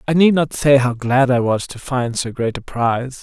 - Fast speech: Yes, fast, 260 wpm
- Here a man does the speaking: Yes, male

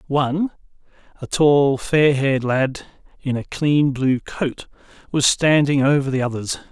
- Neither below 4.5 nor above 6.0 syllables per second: No, 4.2 syllables/s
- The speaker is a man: Yes, male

